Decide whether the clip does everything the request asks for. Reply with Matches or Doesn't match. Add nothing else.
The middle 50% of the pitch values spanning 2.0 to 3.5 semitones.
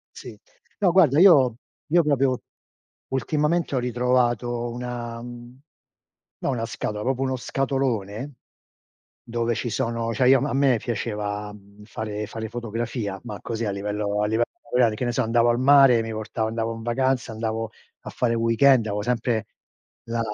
Matches